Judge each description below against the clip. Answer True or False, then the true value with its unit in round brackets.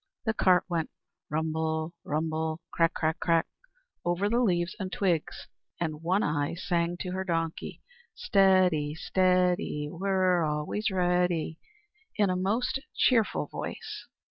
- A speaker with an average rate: False (125 wpm)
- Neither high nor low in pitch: True (175 Hz)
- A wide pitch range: False (3.0 semitones)